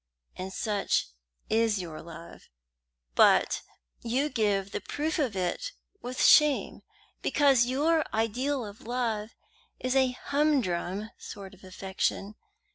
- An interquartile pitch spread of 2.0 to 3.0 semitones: No, wide, 5.5 semitones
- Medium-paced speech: No, slow, 120 wpm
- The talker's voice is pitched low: No, high, 225 Hz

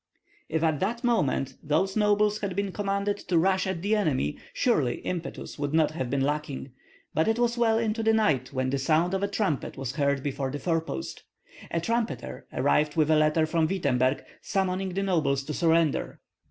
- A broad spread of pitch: Yes, wide, 5.7 semitones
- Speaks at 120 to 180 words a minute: No, average, 190 wpm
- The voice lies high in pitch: No, medium, 165 Hz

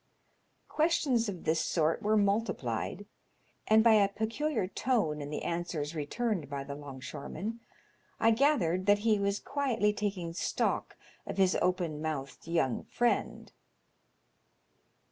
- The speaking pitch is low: No, high, 195 Hz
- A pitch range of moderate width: No, wide, 6.0 semitones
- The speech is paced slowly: Yes, slow, 125 wpm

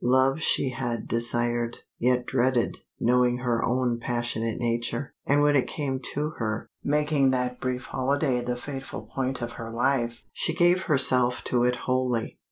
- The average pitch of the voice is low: Yes, low, 125 Hz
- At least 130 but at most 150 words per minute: No, average, 160 wpm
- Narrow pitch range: Yes, narrow, 2.1 semitones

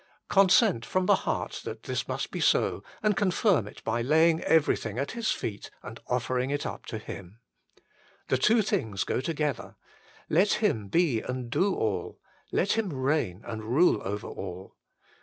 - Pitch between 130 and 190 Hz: Yes, low, 135 Hz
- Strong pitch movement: Yes, wide, 8.5 semitones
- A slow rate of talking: No, average, 165 wpm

